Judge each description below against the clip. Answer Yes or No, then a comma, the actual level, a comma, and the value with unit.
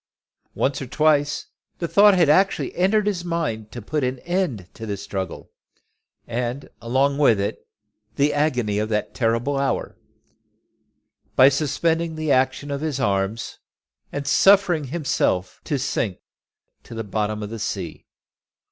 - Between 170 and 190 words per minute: No, average, 145 wpm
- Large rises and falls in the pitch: Yes, wide, 6.1 semitones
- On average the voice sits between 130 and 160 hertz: Yes, low, 135 Hz